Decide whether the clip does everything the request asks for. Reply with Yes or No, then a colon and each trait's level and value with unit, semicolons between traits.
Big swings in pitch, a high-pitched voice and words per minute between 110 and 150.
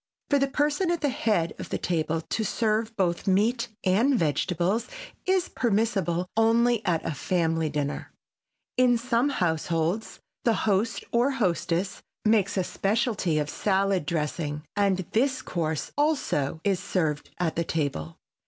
Yes: wide, 6.1 semitones; high, 195 Hz; average, 145 wpm